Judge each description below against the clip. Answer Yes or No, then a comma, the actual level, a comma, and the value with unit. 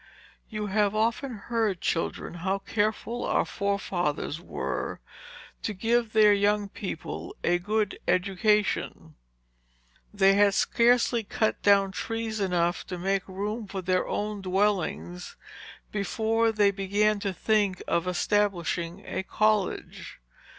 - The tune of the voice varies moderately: No, narrow, 2.3 semitones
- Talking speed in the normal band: No, slow, 120 wpm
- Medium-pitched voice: No, high, 205 Hz